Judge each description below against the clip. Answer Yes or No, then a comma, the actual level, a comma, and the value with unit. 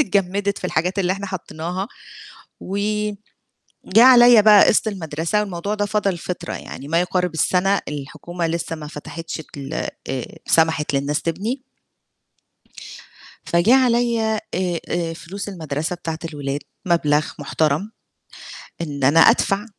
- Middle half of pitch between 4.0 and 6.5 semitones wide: Yes, average, 4.3 semitones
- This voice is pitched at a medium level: Yes, medium, 180 Hz